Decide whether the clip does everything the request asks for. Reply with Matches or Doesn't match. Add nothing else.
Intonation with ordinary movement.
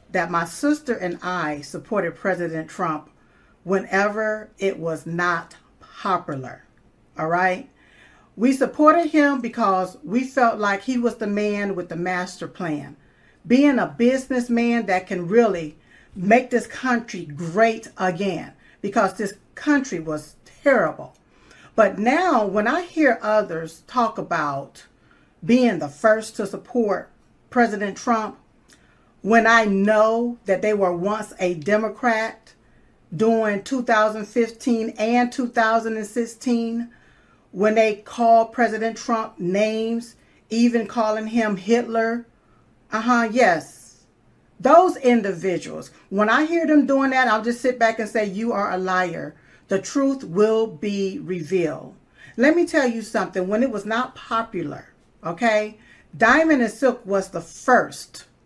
Matches